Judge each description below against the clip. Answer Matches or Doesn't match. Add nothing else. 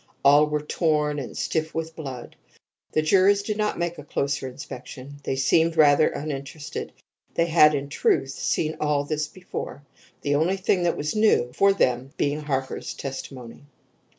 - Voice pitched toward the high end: Doesn't match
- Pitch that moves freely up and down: Doesn't match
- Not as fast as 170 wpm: Matches